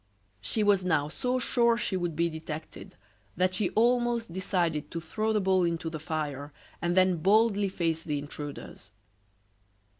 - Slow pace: No, average, 155 wpm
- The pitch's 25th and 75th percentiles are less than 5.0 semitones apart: Yes, average, 4.6 semitones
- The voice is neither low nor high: Yes, medium, 180 Hz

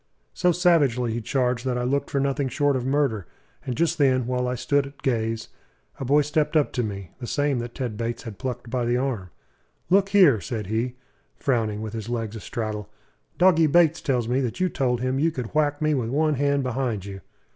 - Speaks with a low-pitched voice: Yes, low, 130 Hz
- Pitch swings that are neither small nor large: Yes, average, 3.7 semitones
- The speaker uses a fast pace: Yes, fast, 215 wpm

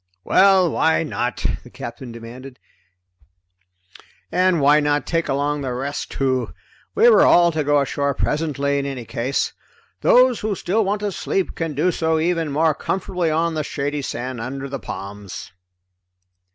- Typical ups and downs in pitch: Yes, average, 3.9 semitones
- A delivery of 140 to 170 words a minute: Yes, average, 155 wpm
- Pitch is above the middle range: No, medium, 145 Hz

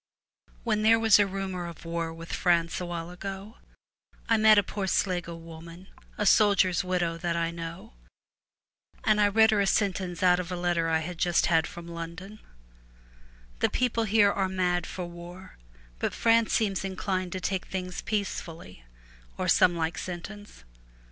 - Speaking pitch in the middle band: Yes, medium, 180 Hz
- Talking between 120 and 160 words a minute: No, average, 170 wpm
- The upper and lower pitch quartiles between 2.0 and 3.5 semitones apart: Yes, average, 3.0 semitones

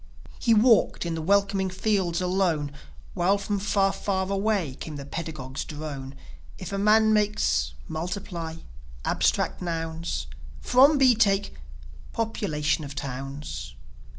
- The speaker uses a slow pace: Yes, slow, 125 wpm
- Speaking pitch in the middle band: Yes, medium, 180 Hz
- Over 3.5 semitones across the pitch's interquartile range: Yes, average, 5.1 semitones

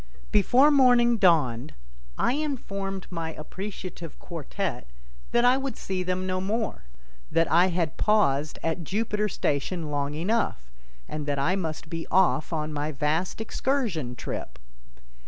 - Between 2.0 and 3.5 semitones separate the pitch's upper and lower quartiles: No, wide, 5.6 semitones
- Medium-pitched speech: Yes, medium, 180 Hz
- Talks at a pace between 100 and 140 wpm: Yes, slow, 135 wpm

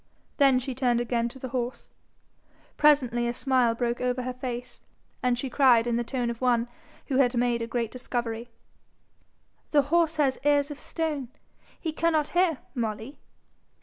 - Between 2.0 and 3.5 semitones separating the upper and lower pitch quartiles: Yes, average, 2.8 semitones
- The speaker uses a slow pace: No, average, 160 wpm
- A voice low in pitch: No, very high, 250 Hz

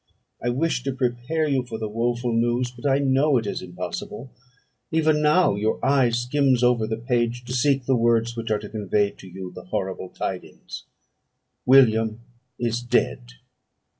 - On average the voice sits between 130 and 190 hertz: No, low, 120 Hz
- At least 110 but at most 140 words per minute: No, average, 165 wpm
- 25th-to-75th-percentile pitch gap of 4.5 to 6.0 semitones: No, average, 3.2 semitones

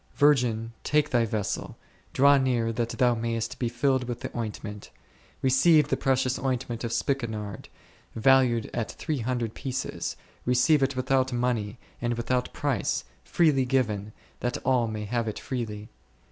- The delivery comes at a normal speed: Yes, average, 155 wpm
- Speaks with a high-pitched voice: No, low, 120 Hz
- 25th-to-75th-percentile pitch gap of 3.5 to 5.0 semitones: No, narrow, 2.6 semitones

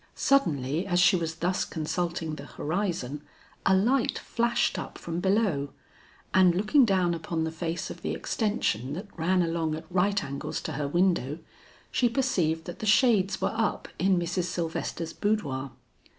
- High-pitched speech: No, medium, 175 Hz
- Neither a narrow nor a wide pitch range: Yes, average, 3.8 semitones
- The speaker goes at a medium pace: Yes, average, 160 wpm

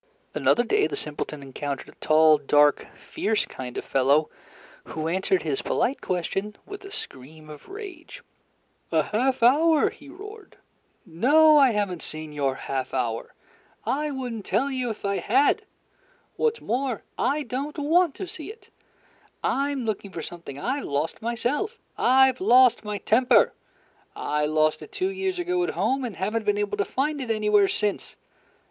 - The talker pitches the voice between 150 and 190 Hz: No, high, 230 Hz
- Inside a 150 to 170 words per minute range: Yes, average, 165 wpm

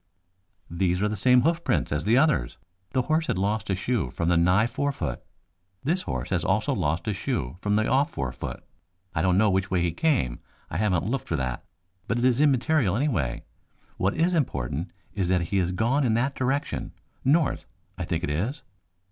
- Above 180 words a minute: Yes, average, 200 wpm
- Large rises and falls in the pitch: Yes, wide, 7.4 semitones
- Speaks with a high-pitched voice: No, low, 105 Hz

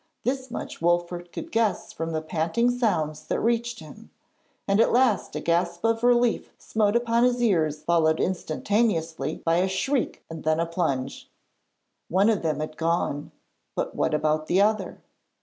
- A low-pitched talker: No, medium, 175 Hz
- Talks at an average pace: Yes, average, 165 wpm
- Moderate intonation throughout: No, wide, 6.2 semitones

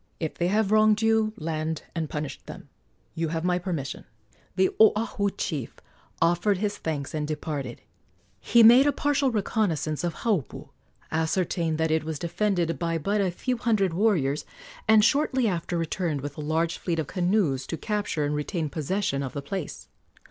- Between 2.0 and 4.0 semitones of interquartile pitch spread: No, average, 5.1 semitones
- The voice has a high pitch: No, medium, 170 Hz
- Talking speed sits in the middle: Yes, average, 170 wpm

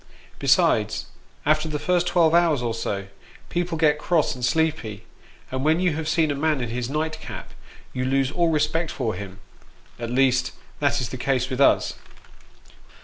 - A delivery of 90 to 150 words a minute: No, average, 170 wpm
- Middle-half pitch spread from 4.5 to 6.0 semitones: No, average, 4.1 semitones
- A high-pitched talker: No, medium, 145 Hz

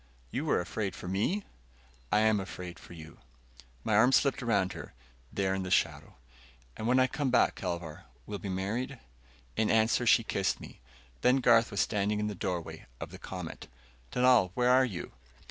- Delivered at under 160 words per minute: No, average, 180 wpm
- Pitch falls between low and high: No, low, 105 Hz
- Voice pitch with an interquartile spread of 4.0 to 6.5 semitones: Yes, average, 4.6 semitones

